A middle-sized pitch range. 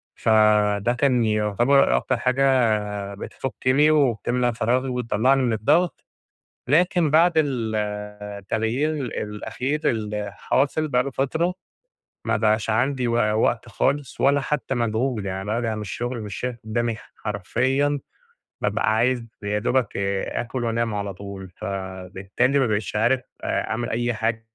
Yes: average, 3.8 semitones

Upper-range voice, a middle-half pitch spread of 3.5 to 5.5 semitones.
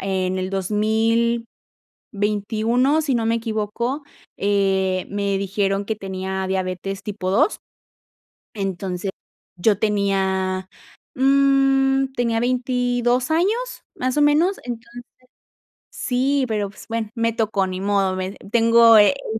Yes: high, 220 Hz; average, 4.1 semitones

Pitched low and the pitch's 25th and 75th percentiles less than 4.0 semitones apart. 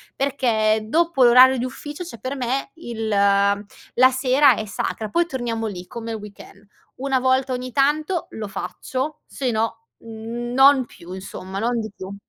No: high, 240 Hz; average, 3.6 semitones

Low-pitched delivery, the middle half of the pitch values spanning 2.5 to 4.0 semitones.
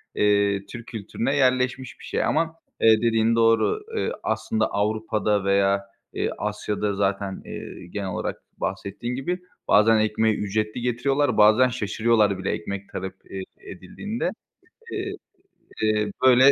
Yes: low, 110 Hz; average, 3.7 semitones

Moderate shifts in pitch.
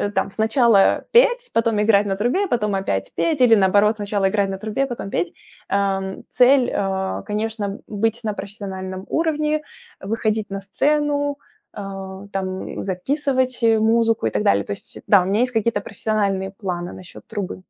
Yes: average, 3.5 semitones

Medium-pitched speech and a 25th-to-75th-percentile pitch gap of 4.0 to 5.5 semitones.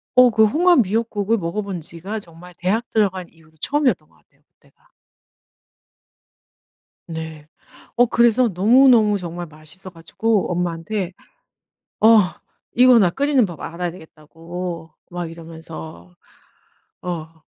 Yes: medium, 180 Hz; average, 5.1 semitones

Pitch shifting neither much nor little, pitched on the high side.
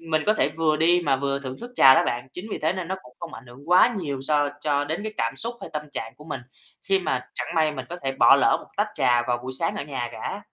No: average, 4.4 semitones; medium, 150 Hz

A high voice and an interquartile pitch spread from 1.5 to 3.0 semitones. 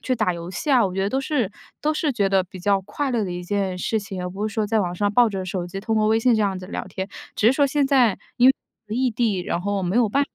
No: high, 205 Hz; average, 4.4 semitones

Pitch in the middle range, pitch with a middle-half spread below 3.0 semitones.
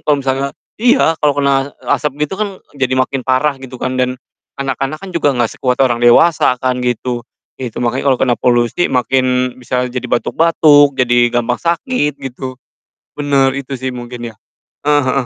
No: low, 130 Hz; narrow, 2.5 semitones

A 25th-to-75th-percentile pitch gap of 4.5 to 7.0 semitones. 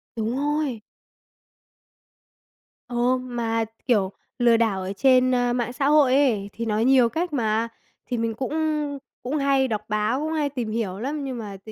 No: average, 3.3 semitones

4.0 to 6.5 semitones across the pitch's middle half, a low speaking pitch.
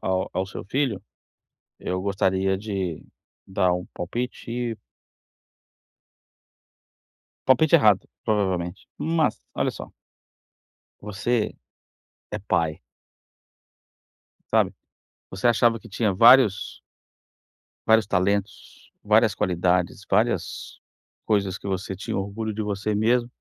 No: average, 3.4 semitones; low, 100 Hz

